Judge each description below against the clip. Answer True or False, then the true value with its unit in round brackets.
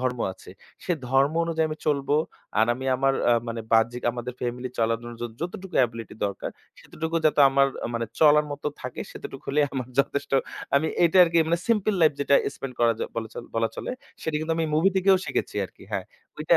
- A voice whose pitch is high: False (140 Hz)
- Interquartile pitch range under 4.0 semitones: False (4.8 semitones)